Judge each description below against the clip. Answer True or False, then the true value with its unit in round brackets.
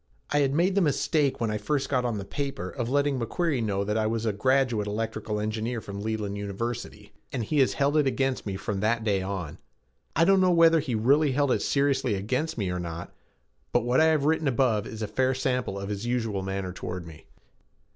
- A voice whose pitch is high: False (120 Hz)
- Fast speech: True (220 wpm)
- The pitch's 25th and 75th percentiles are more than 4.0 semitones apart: True (5.1 semitones)